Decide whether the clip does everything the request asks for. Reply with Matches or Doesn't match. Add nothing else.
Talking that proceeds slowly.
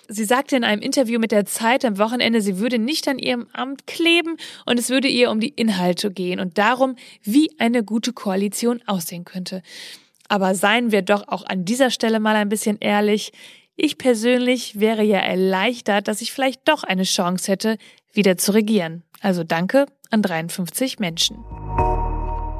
Doesn't match